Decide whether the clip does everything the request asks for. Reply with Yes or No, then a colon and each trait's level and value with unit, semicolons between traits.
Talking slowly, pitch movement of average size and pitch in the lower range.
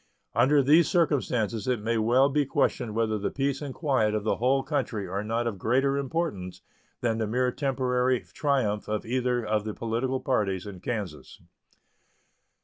No: average, 165 wpm; average, 4.0 semitones; low, 120 Hz